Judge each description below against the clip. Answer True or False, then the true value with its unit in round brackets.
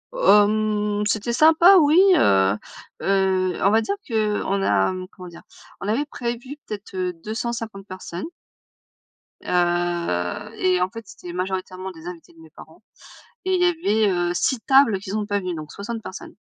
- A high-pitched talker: True (200 Hz)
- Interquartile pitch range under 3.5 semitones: False (3.8 semitones)